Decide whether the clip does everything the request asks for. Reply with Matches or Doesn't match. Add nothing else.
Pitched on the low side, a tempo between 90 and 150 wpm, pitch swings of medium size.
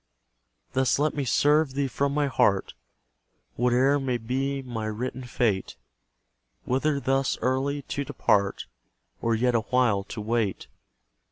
Matches